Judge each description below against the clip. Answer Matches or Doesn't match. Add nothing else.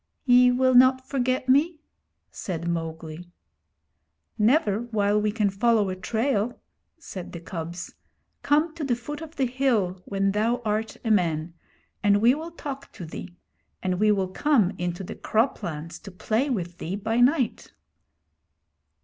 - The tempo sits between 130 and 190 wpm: Matches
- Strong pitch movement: Matches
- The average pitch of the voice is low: Doesn't match